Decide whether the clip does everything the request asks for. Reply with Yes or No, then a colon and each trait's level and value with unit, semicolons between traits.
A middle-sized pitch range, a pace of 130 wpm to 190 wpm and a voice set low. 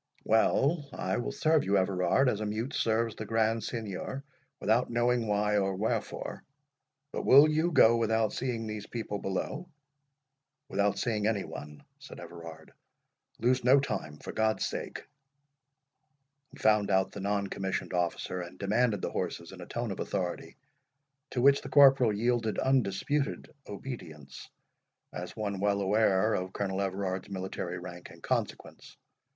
Yes: average, 3.9 semitones; average, 150 wpm; low, 105 Hz